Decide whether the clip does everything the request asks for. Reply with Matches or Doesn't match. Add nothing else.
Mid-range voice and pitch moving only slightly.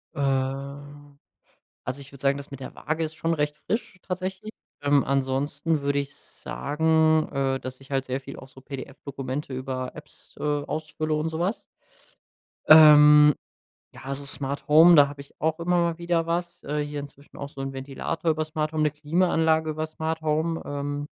Matches